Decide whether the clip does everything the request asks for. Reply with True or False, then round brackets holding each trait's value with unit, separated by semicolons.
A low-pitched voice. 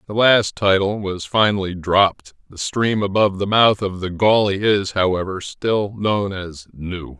True (100 Hz)